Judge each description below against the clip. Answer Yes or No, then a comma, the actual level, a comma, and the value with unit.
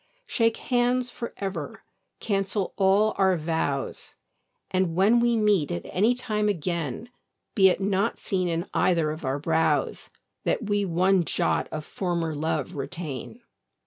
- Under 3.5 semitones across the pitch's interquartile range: No, average, 4.4 semitones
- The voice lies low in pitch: No, high, 190 Hz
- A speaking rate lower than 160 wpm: Yes, average, 145 wpm